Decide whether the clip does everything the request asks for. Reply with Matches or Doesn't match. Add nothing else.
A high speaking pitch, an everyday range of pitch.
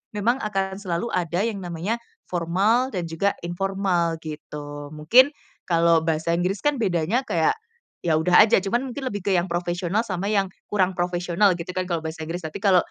Doesn't match